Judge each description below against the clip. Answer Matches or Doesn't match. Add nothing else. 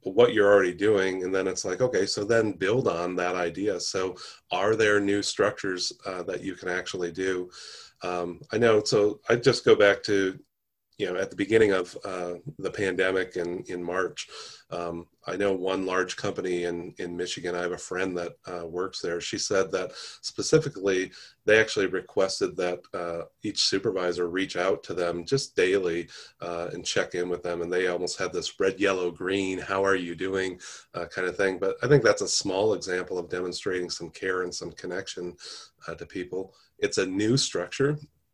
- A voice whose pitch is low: Matches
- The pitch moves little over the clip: Matches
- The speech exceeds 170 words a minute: Matches